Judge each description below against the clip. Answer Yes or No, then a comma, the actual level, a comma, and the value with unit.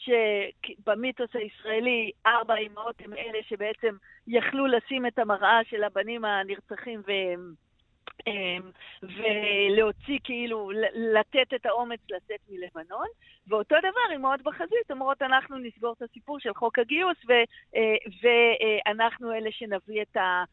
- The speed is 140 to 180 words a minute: No, average, 115 wpm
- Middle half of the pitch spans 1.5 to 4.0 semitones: Yes, average, 2.8 semitones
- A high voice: Yes, high, 225 Hz